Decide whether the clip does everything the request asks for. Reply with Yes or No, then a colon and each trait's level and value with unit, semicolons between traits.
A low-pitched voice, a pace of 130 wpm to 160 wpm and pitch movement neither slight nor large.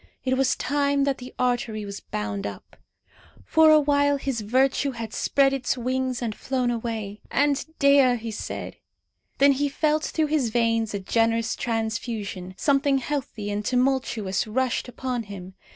No: very high, 250 Hz; average, 155 wpm; average, 3.9 semitones